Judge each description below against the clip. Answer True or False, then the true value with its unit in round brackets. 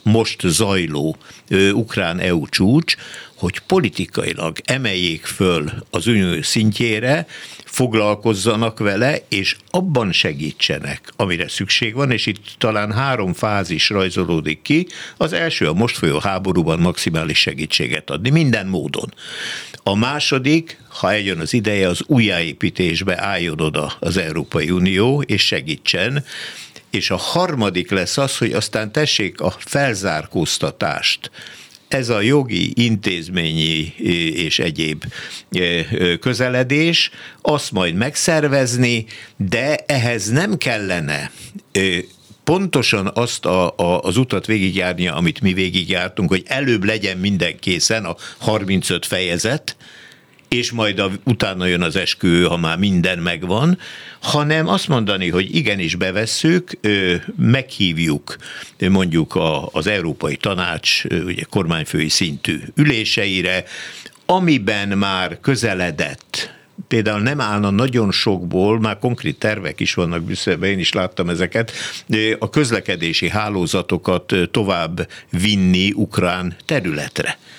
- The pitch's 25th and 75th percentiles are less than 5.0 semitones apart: False (5.5 semitones)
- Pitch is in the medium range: False (105 Hz)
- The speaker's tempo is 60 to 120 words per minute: True (110 wpm)